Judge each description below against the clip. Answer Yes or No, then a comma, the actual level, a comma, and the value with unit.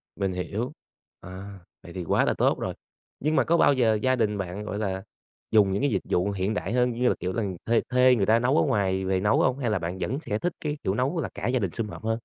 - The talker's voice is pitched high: No, low, 110 Hz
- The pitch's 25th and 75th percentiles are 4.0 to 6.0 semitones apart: Yes, average, 4.6 semitones